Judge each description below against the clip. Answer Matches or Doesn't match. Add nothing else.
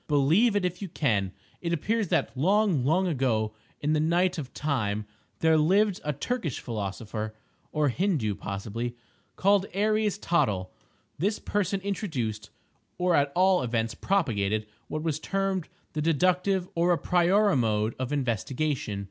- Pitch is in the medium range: Matches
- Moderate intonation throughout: Doesn't match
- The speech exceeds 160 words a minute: Doesn't match